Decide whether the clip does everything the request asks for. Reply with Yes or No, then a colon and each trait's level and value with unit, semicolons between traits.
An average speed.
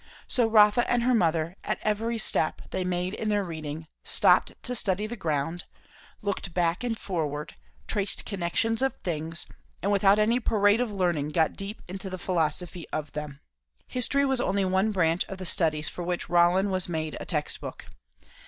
Yes: average, 180 wpm